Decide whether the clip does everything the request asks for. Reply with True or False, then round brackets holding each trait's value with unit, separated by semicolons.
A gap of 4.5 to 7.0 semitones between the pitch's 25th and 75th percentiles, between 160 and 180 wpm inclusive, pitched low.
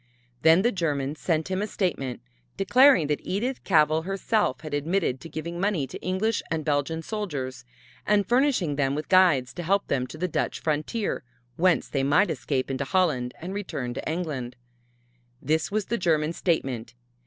False (5.1 semitones; 165 wpm; 160 Hz)